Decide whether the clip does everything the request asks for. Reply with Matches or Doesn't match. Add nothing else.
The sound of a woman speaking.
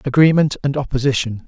Doesn't match